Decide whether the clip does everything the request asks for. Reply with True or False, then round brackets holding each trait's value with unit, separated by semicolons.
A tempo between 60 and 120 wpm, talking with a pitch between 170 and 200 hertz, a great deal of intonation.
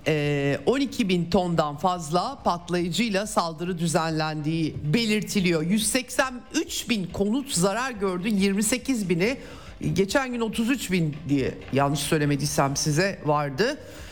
True (100 wpm; 185 Hz; 6.5 semitones)